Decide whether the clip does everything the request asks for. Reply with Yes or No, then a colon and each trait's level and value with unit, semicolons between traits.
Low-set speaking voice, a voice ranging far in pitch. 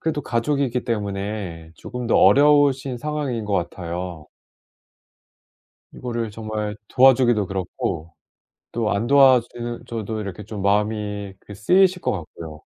No: low, 110 Hz; average, 4.3 semitones